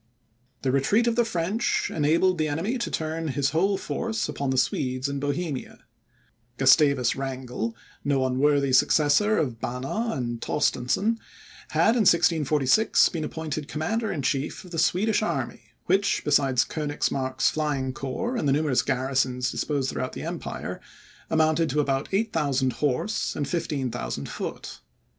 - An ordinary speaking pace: Yes, average, 145 wpm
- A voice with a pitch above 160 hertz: No, medium, 145 Hz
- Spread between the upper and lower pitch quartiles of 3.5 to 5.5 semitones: Yes, average, 4.3 semitones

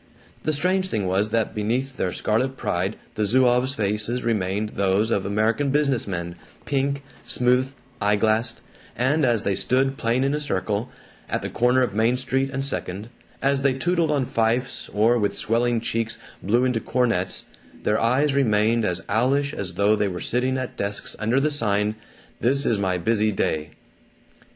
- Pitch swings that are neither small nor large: Yes, average, 4.2 semitones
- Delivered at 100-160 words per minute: No, average, 170 wpm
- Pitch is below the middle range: Yes, low, 115 Hz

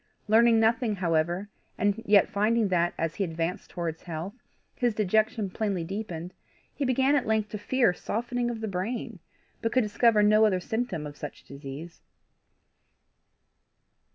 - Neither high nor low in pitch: No, high, 210 Hz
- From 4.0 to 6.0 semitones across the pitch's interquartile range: Yes, average, 4.5 semitones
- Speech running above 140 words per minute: Yes, average, 150 wpm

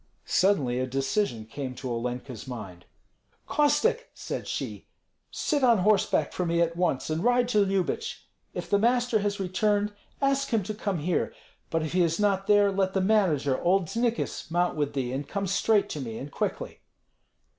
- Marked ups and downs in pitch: Yes, wide, 6.9 semitones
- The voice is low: No, medium, 185 Hz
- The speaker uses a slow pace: No, average, 175 wpm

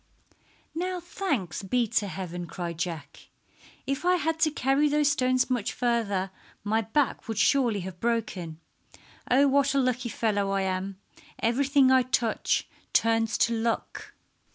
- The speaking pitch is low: No, high, 235 Hz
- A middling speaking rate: Yes, average, 150 wpm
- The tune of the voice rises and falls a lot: Yes, wide, 5.8 semitones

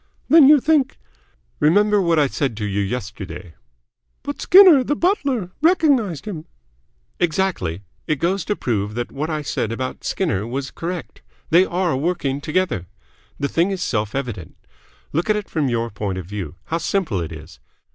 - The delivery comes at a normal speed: Yes, average, 170 wpm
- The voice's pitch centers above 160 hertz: No, medium, 155 Hz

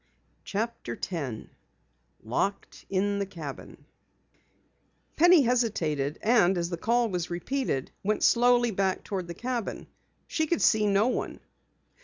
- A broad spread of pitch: Yes, wide, 5.7 semitones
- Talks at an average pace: No, slow, 125 wpm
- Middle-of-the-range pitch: No, high, 200 Hz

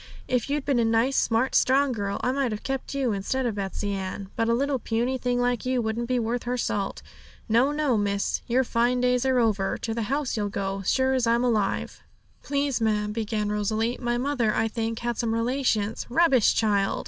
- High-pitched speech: Yes, high, 235 Hz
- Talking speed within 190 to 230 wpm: Yes, fast, 205 wpm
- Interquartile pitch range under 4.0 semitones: Yes, average, 3.1 semitones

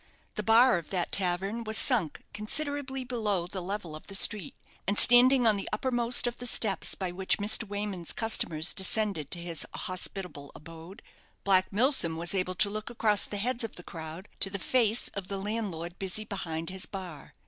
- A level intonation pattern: No, average, 4.0 semitones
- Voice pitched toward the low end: No, high, 200 Hz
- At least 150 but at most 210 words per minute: Yes, average, 185 wpm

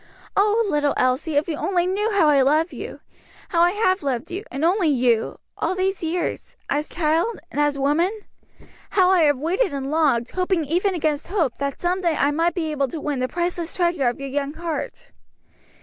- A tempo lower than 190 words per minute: No, average, 200 wpm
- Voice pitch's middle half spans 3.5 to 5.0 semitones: Yes, average, 4.1 semitones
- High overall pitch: Yes, very high, 320 Hz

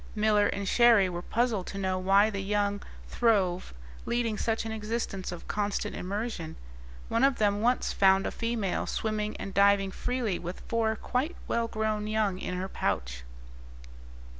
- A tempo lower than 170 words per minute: Yes, average, 160 wpm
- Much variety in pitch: No, average, 2.8 semitones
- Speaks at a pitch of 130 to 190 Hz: No, high, 210 Hz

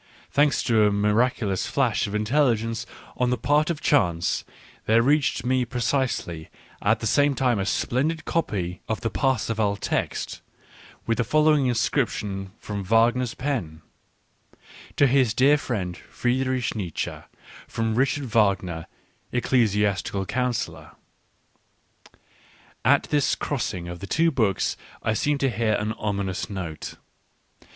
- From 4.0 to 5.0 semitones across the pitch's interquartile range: Yes, average, 4.5 semitones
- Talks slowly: Yes, slow, 130 wpm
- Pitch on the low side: Yes, low, 115 Hz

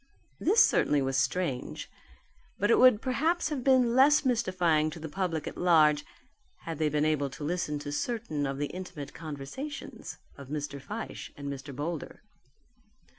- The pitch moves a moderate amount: No, wide, 8.2 semitones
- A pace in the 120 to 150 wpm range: No, average, 160 wpm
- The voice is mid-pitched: Yes, medium, 160 Hz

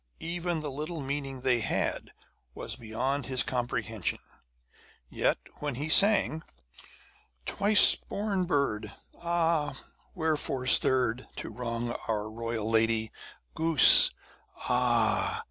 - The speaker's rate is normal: No, slow, 105 wpm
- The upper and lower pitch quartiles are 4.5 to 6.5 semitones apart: Yes, average, 5.3 semitones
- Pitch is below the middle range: Yes, low, 130 Hz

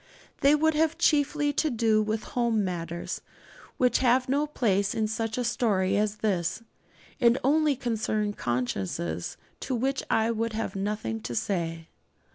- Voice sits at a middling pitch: No, high, 220 Hz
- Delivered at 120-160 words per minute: Yes, average, 150 wpm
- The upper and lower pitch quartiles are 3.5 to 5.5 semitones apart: Yes, average, 5.0 semitones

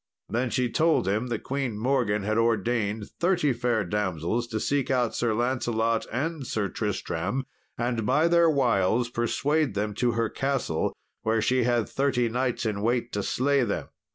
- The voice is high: No, low, 120 Hz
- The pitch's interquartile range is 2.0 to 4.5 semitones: Yes, average, 3.3 semitones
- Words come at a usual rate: Yes, average, 165 wpm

